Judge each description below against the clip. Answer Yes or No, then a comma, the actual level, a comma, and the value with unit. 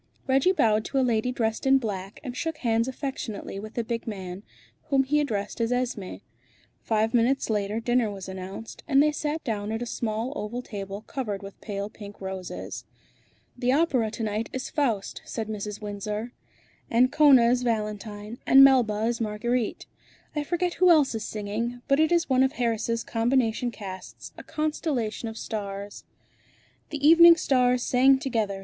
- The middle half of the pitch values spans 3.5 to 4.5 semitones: Yes, average, 4.0 semitones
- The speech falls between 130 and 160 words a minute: No, average, 170 wpm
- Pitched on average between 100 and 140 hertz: No, high, 230 Hz